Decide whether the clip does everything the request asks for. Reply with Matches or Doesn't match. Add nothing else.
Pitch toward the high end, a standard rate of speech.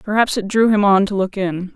Doesn't match